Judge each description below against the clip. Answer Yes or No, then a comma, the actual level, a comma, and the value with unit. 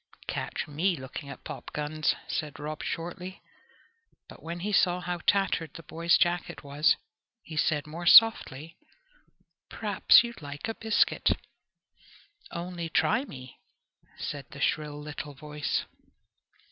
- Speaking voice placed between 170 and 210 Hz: No, medium, 155 Hz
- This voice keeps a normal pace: No, slow, 125 wpm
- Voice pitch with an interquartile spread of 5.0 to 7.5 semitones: No, average, 3.1 semitones